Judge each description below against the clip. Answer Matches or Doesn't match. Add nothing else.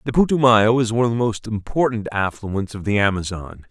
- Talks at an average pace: Matches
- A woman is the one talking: Doesn't match